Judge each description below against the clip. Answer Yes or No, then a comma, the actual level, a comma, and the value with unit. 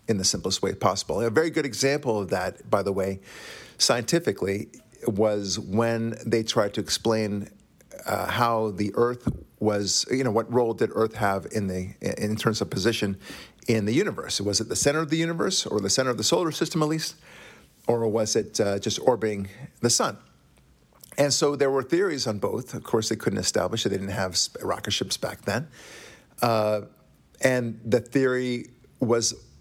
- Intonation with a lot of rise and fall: No, average, 3.5 semitones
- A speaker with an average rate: Yes, average, 185 wpm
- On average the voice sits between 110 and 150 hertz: Yes, low, 115 Hz